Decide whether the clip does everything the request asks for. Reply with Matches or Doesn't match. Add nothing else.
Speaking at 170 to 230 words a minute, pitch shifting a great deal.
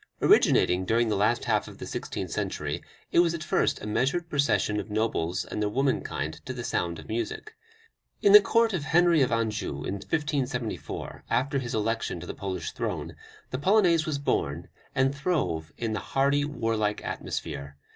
Matches